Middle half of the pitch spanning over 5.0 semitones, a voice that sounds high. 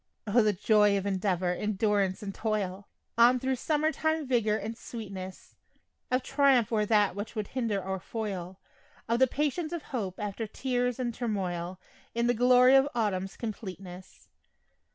No: average, 4.2 semitones; high, 215 Hz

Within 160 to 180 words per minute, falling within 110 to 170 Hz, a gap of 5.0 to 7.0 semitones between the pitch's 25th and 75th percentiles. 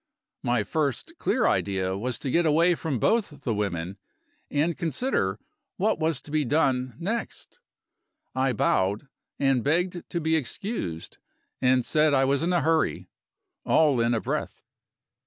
No: average, 150 wpm; medium, 140 Hz; wide, 5.6 semitones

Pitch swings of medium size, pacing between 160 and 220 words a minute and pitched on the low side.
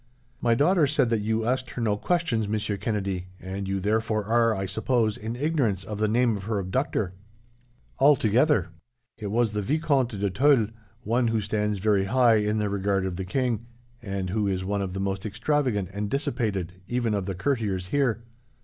Yes: average, 3.6 semitones; average, 185 wpm; low, 110 Hz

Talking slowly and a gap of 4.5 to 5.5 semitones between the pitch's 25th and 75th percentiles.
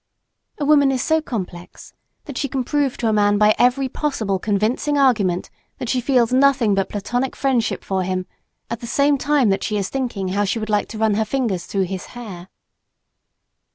No: average, 195 wpm; average, 5.0 semitones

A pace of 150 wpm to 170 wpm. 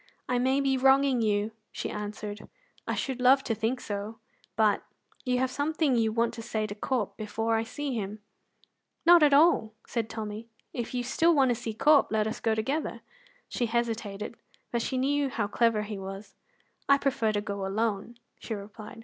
No: average, 185 wpm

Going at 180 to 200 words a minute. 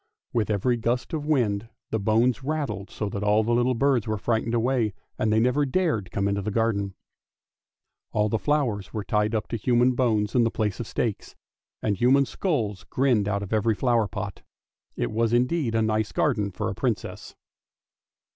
Yes: average, 185 wpm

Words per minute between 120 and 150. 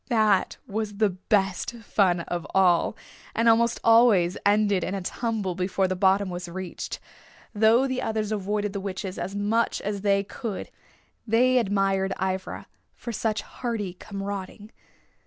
Yes: average, 145 wpm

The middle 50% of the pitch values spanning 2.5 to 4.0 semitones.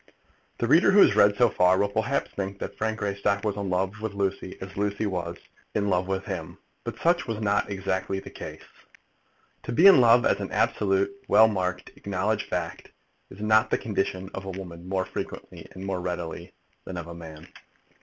Yes: average, 2.8 semitones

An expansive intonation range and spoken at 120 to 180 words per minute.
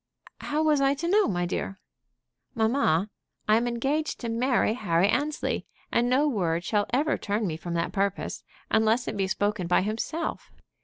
Yes: wide, 6.1 semitones; average, 170 wpm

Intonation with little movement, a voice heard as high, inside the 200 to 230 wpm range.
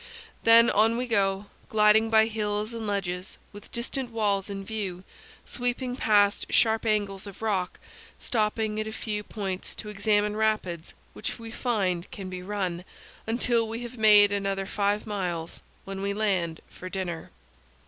No: narrow, 2.3 semitones; high, 210 Hz; average, 155 wpm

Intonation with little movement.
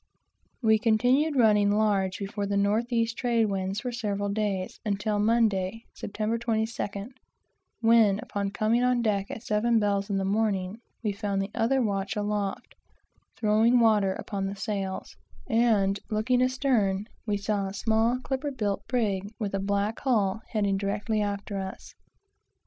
Yes: narrow, 2.3 semitones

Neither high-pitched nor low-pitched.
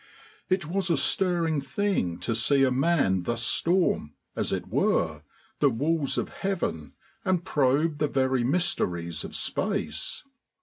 Yes: medium, 145 Hz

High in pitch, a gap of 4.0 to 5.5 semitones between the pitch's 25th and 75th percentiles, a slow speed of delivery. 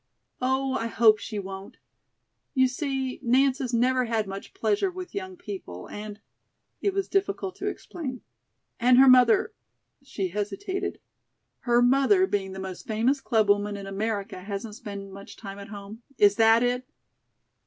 No: high, 230 Hz; average, 4.7 semitones; average, 155 wpm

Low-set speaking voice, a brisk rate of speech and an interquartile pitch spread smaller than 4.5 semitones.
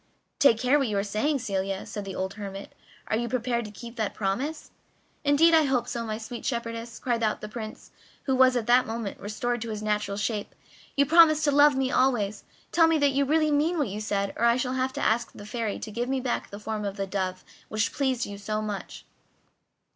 No: high, 235 Hz; fast, 225 wpm; average, 4.0 semitones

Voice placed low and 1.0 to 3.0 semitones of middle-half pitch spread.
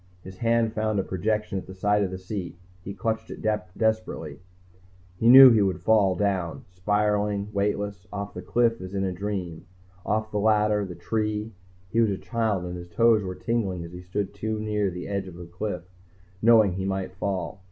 Yes: low, 100 Hz; average, 2.7 semitones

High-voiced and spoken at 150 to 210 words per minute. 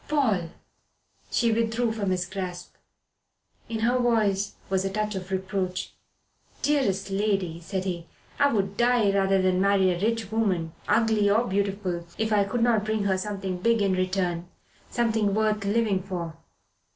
Yes: high, 200 Hz; average, 155 wpm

